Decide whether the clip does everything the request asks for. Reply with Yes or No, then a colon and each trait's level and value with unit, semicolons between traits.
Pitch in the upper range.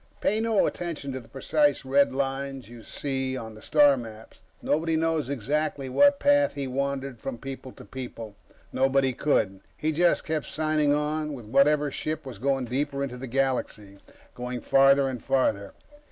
No: low, 135 Hz